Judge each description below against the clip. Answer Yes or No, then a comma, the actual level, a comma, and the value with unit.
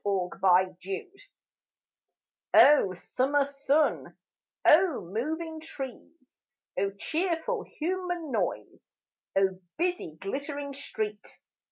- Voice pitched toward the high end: Yes, very high, 285 Hz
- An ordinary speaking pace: No, slow, 70 wpm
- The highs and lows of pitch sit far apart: Yes, wide, 7.3 semitones